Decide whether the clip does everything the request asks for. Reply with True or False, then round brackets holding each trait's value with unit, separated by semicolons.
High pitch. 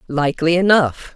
False (165 Hz)